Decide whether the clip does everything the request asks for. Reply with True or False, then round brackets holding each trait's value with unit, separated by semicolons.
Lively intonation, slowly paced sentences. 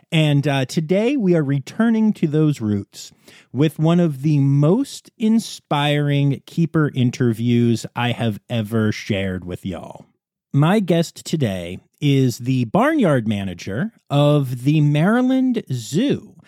True (6.3 semitones; 125 wpm)